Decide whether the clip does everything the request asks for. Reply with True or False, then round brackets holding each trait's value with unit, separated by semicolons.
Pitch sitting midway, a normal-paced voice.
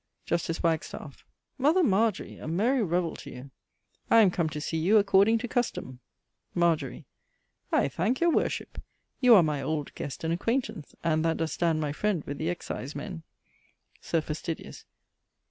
True (170 Hz; 160 wpm)